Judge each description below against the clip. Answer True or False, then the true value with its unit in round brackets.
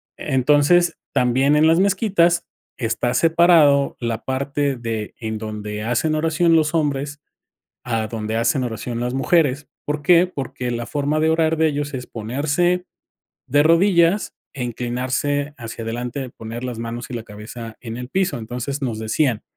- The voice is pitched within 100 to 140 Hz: True (135 Hz)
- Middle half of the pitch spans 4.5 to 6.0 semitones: True (5.0 semitones)